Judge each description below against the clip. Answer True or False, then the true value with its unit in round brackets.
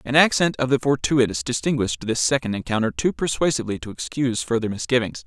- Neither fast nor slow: True (170 wpm)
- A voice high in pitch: False (120 Hz)